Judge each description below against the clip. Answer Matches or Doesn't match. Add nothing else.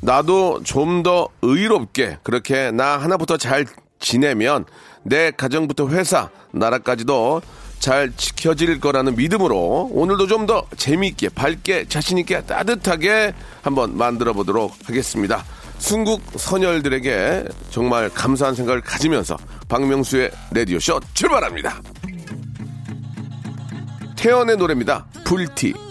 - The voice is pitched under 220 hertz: Matches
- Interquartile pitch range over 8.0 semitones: Doesn't match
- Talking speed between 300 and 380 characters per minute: Doesn't match